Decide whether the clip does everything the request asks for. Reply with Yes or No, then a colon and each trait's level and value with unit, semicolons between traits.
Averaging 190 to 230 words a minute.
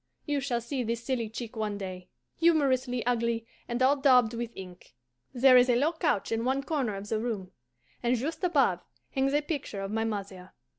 Yes: average, 195 wpm